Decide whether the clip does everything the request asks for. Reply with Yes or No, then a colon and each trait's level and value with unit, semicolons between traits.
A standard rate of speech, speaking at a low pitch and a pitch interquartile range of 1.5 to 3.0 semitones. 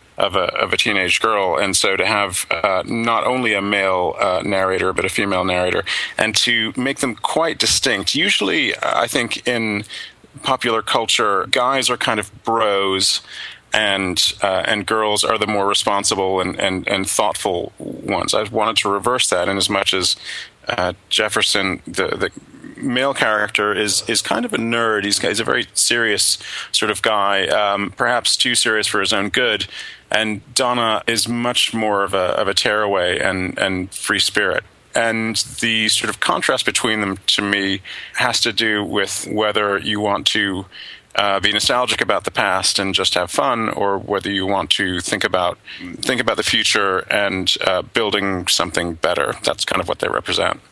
Yes: average, 180 wpm; low, 105 Hz; average, 2.7 semitones